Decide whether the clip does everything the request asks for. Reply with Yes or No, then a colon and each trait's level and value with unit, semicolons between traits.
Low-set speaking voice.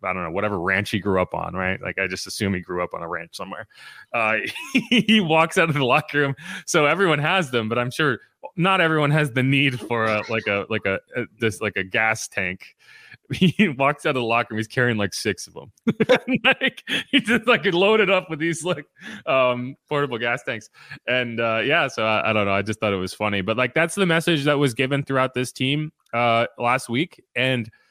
Yes: low, 130 Hz